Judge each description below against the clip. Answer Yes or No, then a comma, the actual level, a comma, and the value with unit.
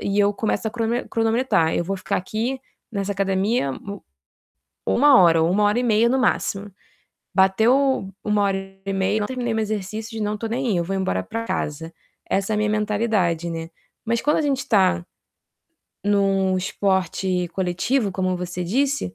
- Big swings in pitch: No, average, 3.4 semitones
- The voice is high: Yes, high, 205 Hz